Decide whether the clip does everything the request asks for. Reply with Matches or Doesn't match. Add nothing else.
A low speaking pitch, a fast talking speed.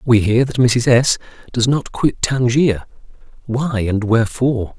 Doesn't match